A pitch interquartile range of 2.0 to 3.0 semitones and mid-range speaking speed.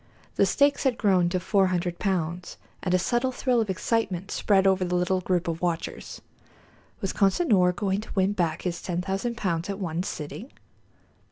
Yes: narrow, 2.6 semitones; average, 180 wpm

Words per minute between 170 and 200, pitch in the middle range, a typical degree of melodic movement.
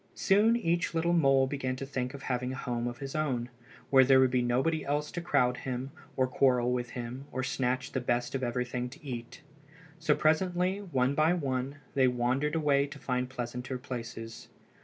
No: average, 190 wpm; low, 130 Hz; average, 3.1 semitones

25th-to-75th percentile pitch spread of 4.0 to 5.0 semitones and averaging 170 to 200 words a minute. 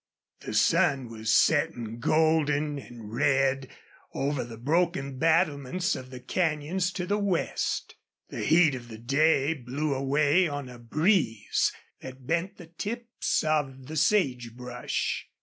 No: average, 4.3 semitones; slow, 135 wpm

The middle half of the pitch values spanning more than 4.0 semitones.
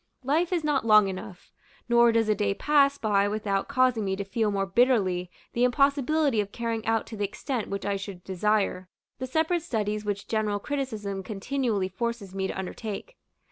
Yes: average, 4.4 semitones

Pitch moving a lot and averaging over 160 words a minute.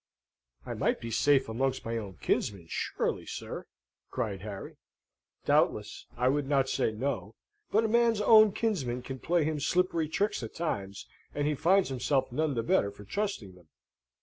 Yes: wide, 7.3 semitones; average, 170 wpm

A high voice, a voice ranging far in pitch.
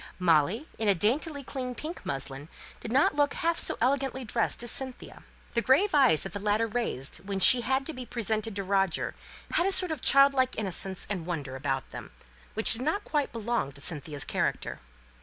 Yes: high, 230 Hz; wide, 6.5 semitones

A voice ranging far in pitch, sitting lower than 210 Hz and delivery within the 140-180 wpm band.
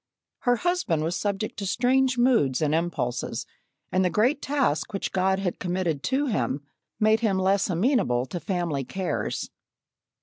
Yes: wide, 6.6 semitones; high, 190 Hz; average, 155 wpm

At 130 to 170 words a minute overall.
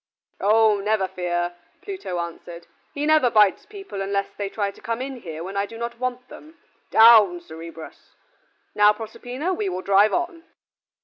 Yes: average, 165 wpm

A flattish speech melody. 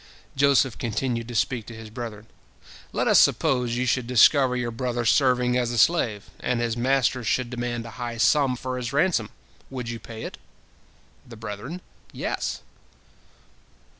Yes: narrow, 1.8 semitones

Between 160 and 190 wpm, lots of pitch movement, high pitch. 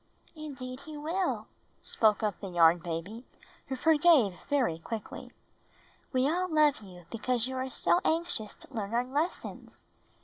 No: average, 145 wpm; wide, 6.6 semitones; very high, 255 Hz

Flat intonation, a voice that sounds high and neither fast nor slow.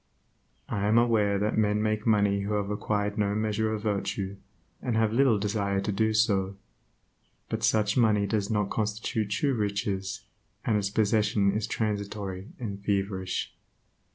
No: narrow, 1.5 semitones; low, 105 Hz; average, 155 wpm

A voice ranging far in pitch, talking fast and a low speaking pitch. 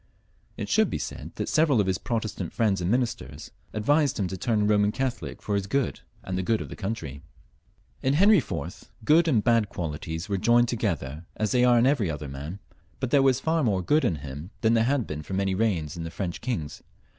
Yes: wide, 6.0 semitones; fast, 220 wpm; low, 105 Hz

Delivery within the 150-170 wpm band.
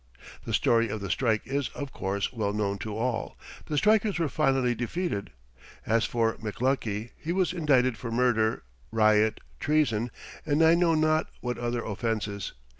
Yes: average, 160 wpm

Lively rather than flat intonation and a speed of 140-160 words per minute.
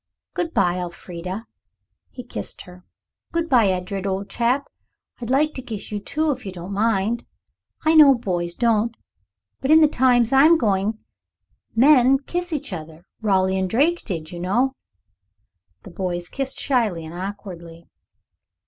Yes: wide, 6.5 semitones; average, 155 wpm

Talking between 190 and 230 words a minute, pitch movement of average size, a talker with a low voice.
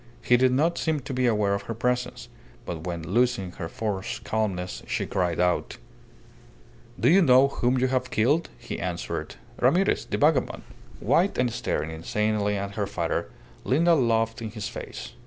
No: average, 170 wpm; average, 4.5 semitones; low, 115 Hz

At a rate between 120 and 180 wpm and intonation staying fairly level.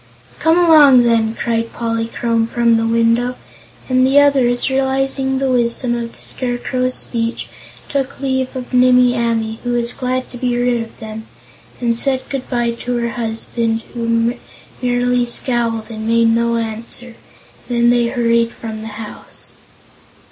Yes: average, 155 wpm; narrow, 1.7 semitones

